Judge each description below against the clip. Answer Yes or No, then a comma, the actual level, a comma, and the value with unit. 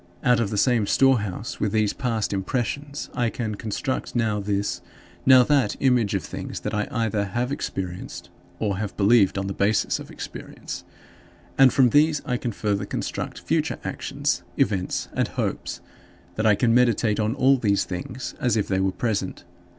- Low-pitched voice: Yes, low, 110 Hz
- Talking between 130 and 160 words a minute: No, average, 175 wpm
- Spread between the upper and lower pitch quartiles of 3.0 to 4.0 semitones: Yes, average, 3.6 semitones